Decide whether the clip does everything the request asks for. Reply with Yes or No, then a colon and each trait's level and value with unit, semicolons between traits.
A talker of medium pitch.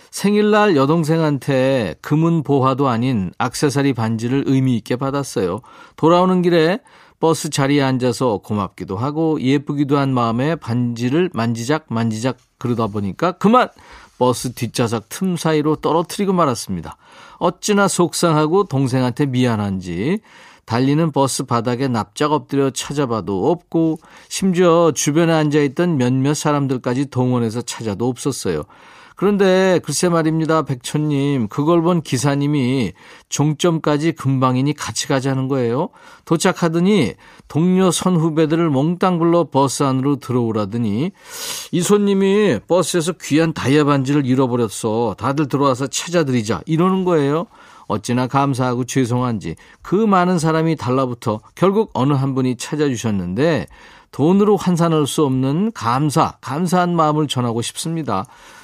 Yes: medium, 145 Hz